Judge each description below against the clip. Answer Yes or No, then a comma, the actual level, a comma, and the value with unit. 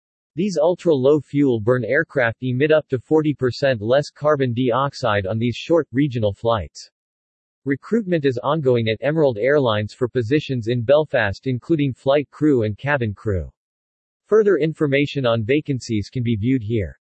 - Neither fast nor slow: Yes, average, 145 wpm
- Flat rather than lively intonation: No, average, 4.3 semitones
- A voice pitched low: Yes, low, 130 Hz